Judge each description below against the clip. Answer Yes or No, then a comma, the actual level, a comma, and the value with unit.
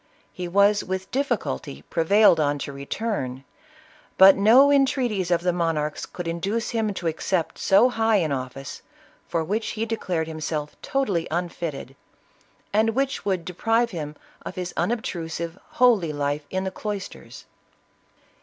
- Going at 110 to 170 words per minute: Yes, average, 145 wpm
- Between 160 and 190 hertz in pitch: Yes, medium, 185 Hz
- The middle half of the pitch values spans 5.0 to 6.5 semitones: Yes, wide, 5.4 semitones